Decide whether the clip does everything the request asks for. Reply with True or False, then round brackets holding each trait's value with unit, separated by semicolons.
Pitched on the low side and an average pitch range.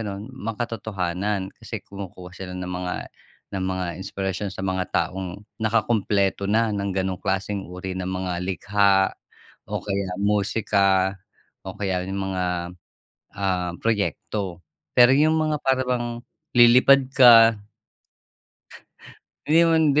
True (100 Hz; 3.1 semitones)